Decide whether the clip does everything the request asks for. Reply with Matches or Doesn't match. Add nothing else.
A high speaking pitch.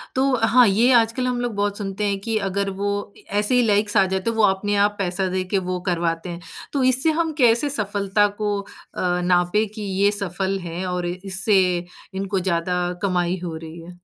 Matches